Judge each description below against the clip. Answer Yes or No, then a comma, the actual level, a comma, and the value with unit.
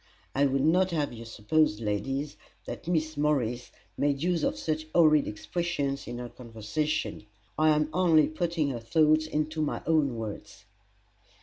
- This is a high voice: No, medium, 150 Hz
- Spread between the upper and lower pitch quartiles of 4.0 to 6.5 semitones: Yes, average, 4.4 semitones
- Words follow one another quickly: No, average, 150 wpm